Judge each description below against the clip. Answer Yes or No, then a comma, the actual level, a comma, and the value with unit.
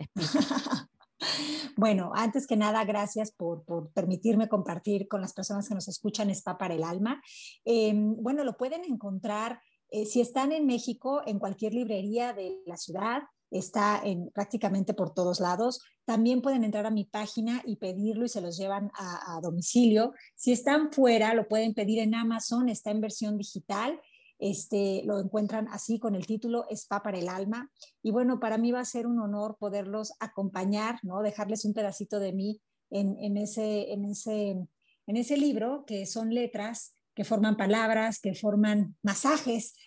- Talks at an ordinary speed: Yes, average, 170 wpm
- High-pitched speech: Yes, high, 215 Hz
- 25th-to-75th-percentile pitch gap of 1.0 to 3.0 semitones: Yes, average, 2.7 semitones